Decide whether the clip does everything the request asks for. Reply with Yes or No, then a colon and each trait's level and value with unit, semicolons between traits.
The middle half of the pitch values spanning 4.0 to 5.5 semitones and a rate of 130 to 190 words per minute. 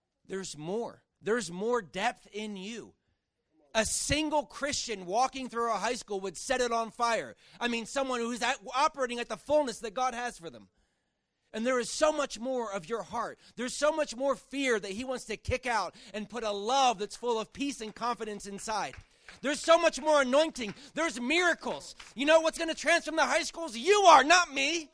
No: average, 4.7 semitones; fast, 205 wpm